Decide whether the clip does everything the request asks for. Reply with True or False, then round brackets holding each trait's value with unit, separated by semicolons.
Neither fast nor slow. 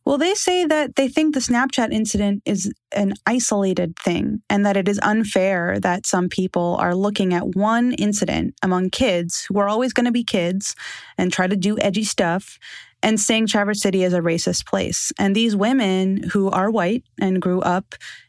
True (190 wpm)